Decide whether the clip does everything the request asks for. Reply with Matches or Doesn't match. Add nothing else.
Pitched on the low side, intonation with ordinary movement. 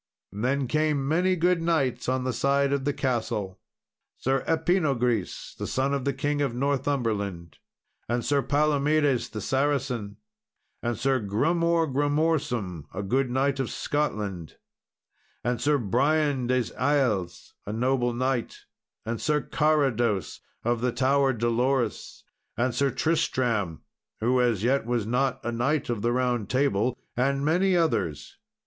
Matches